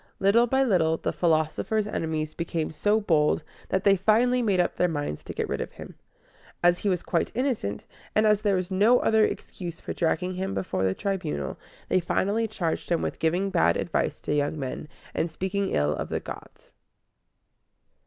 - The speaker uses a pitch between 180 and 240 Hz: Yes, medium, 185 Hz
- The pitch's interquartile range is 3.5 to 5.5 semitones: Yes, average, 4.4 semitones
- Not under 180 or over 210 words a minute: Yes, average, 185 wpm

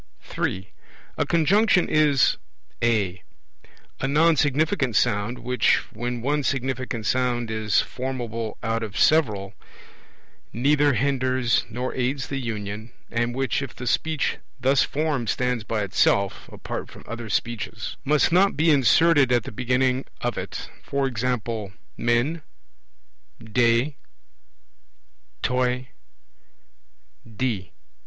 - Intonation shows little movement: No, average, 3.4 semitones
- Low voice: Yes, low, 125 Hz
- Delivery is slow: Yes, slow, 115 wpm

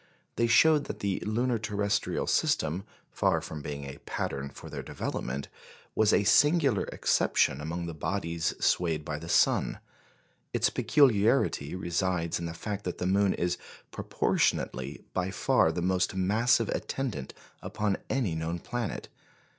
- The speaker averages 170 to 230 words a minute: No, average, 145 wpm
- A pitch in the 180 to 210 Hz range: No, very low, 95 Hz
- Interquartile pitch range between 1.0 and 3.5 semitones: No, average, 5.0 semitones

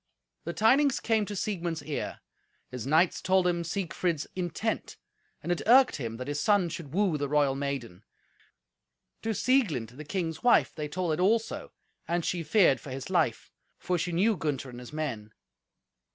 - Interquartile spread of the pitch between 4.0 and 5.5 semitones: Yes, average, 5.2 semitones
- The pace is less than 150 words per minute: No, average, 170 wpm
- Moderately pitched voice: Yes, medium, 165 Hz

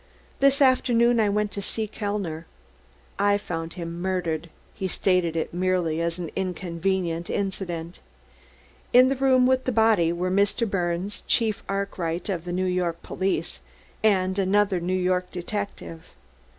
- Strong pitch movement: No, average, 3.2 semitones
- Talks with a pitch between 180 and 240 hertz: Yes, medium, 185 Hz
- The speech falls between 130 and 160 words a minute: Yes, average, 150 wpm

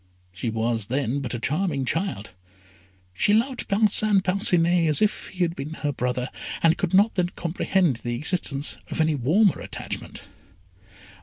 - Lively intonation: Yes, wide, 6.8 semitones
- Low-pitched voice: No, medium, 160 Hz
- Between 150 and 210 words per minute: Yes, average, 155 wpm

